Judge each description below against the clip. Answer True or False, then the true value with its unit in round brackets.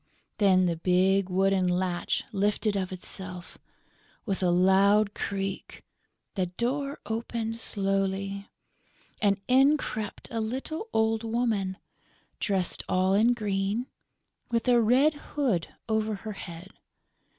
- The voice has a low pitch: False (200 Hz)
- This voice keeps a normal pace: False (115 wpm)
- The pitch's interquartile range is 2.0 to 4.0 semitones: True (3.2 semitones)